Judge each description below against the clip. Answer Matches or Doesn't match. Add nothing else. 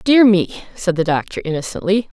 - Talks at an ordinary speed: Matches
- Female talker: Matches